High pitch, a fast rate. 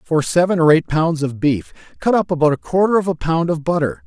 No: medium, 155 Hz; fast, 250 wpm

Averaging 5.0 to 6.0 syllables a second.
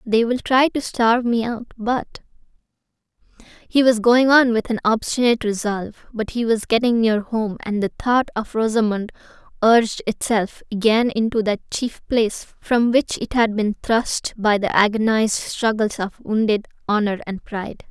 No: 4.8 syllables/s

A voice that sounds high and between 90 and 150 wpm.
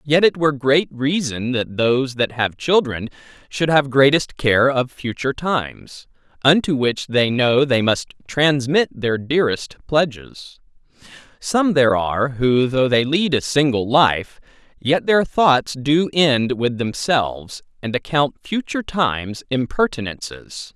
No: low, 135 Hz; average, 140 wpm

